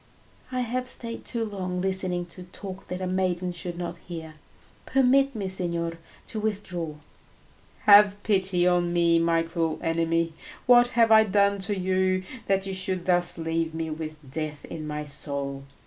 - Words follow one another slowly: No, average, 165 wpm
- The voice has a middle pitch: Yes, medium, 180 Hz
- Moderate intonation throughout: Yes, average, 3.3 semitones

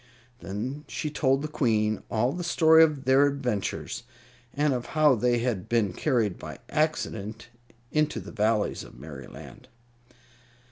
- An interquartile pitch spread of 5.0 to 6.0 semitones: Yes, wide, 5.4 semitones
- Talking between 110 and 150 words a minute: Yes, average, 140 wpm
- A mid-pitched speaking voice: No, low, 130 Hz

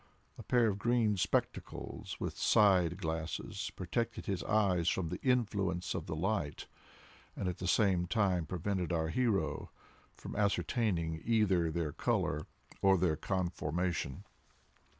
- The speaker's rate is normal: No, slow, 130 wpm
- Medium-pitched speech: No, very low, 90 Hz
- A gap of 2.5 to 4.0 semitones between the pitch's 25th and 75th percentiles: Yes, average, 3.7 semitones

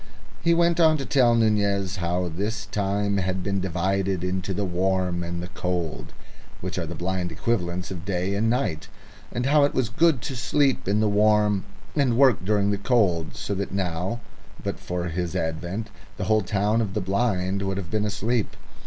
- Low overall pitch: Yes, low, 100 Hz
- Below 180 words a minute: No, average, 190 wpm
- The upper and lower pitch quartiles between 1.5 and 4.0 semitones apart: Yes, average, 3.5 semitones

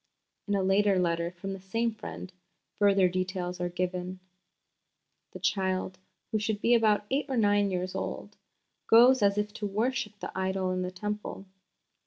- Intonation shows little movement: Yes, narrow, 2.2 semitones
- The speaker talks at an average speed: Yes, average, 165 wpm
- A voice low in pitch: No, high, 195 Hz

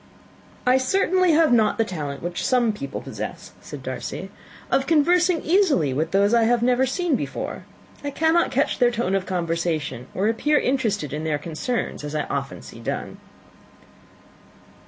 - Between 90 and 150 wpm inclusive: No, average, 160 wpm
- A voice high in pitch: Yes, high, 230 Hz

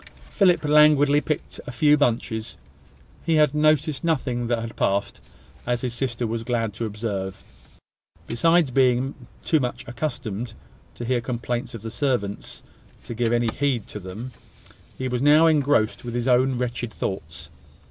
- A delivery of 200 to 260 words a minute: No, average, 155 wpm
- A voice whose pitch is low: Yes, low, 120 Hz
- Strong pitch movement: No, average, 4.0 semitones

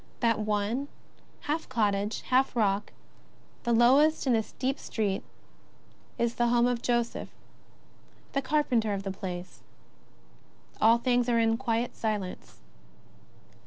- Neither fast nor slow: No, slow, 125 wpm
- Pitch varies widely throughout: No, average, 2.7 semitones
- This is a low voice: No, high, 235 Hz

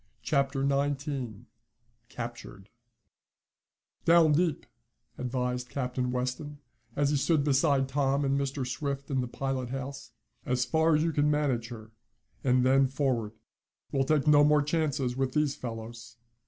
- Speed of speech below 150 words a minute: Yes, average, 140 wpm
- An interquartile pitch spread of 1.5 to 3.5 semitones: Yes, narrow, 2.6 semitones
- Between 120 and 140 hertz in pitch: Yes, low, 135 Hz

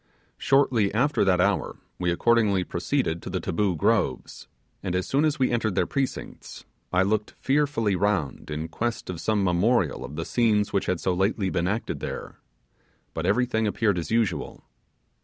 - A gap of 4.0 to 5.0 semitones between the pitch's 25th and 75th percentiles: Yes, average, 4.6 semitones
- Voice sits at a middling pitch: No, low, 100 Hz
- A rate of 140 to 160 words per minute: No, average, 170 wpm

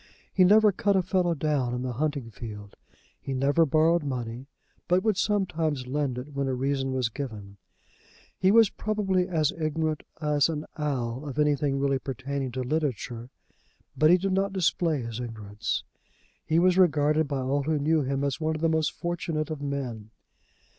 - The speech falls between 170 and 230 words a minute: Yes, average, 175 wpm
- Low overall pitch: No, medium, 145 Hz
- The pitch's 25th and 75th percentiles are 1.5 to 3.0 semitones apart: No, average, 4.2 semitones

